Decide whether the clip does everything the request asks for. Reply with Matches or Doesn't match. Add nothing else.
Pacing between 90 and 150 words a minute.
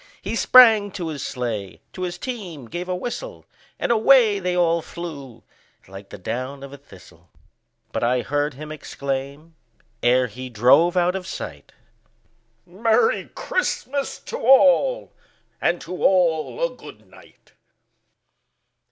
Matches